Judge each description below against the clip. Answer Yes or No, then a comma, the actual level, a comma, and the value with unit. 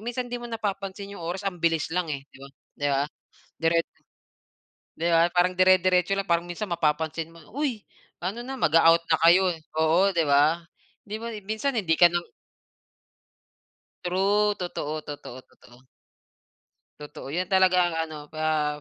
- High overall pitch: No, medium, 175 Hz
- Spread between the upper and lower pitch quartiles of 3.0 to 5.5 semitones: Yes, average, 3.6 semitones